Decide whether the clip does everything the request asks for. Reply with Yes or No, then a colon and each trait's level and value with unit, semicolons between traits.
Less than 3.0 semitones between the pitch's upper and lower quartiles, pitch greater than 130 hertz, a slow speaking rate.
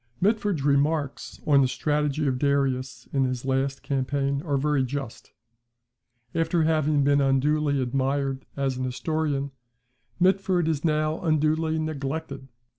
Yes: narrow, 2.5 semitones; medium, 140 Hz; slow, 125 wpm